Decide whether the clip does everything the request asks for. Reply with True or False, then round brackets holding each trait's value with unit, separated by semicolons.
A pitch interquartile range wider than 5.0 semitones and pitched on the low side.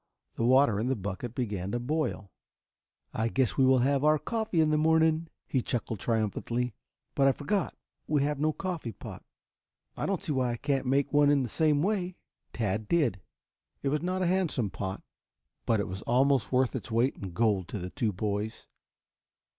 True (5.6 semitones; 130 Hz)